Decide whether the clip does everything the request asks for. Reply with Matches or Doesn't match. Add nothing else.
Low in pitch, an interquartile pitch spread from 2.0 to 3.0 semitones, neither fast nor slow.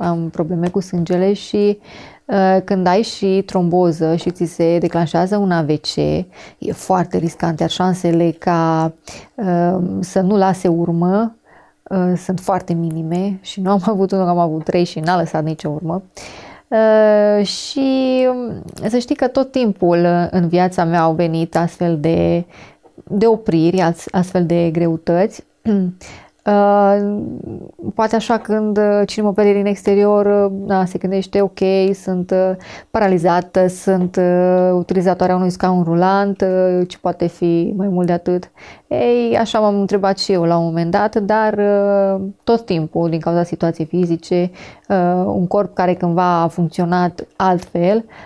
Doesn't match